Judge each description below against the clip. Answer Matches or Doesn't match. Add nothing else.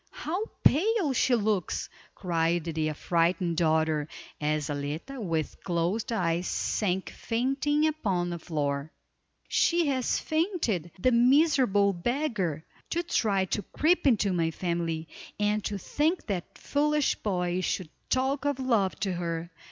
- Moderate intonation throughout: Doesn't match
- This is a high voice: Matches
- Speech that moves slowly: Matches